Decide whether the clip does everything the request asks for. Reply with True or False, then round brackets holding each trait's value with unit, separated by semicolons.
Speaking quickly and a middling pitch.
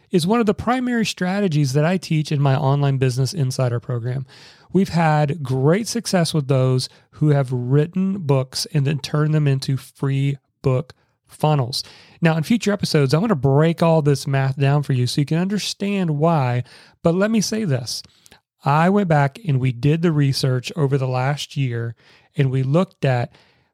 False (180 wpm; 145 Hz)